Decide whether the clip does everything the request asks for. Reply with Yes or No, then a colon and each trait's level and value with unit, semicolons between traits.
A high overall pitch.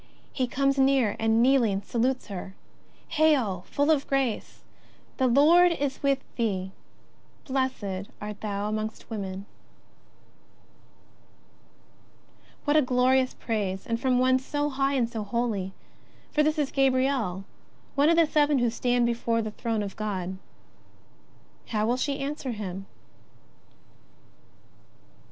Yes: high, 245 Hz